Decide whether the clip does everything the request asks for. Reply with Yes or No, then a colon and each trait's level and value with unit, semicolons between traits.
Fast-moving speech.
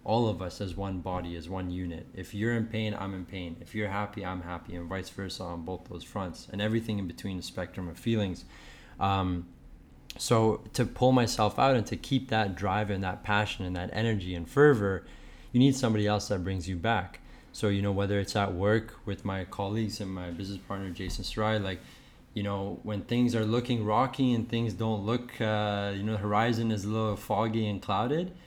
Yes: fast, 215 wpm